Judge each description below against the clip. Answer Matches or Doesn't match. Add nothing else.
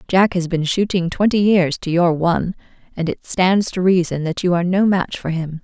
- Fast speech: Matches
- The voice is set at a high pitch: Doesn't match